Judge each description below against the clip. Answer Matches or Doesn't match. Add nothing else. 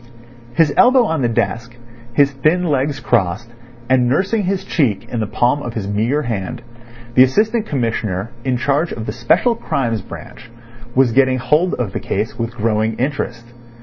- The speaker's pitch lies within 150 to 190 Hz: Doesn't match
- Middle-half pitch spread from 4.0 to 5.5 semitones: Matches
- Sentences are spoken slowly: Doesn't match